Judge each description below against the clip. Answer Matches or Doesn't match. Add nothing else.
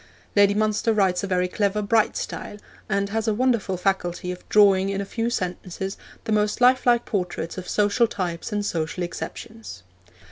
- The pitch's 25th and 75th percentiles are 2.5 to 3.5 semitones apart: Matches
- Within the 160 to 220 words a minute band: Matches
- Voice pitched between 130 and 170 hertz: Doesn't match